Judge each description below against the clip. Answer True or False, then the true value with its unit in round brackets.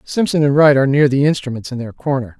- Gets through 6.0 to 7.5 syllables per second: True (6.6 syllables/s)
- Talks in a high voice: False (140 Hz)